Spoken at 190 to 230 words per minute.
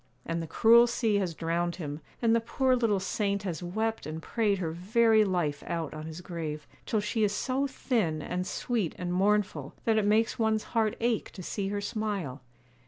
Yes: average, 195 wpm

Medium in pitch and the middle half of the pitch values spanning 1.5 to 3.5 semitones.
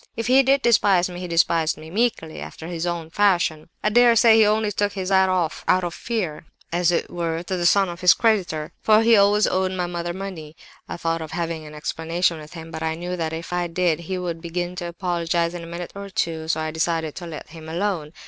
Yes: medium, 175 Hz; average, 2.8 semitones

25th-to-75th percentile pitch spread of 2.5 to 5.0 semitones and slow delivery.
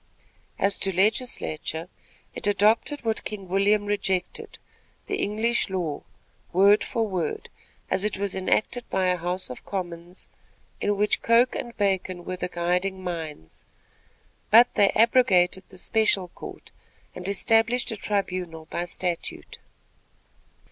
Yes: average, 2.9 semitones; slow, 130 wpm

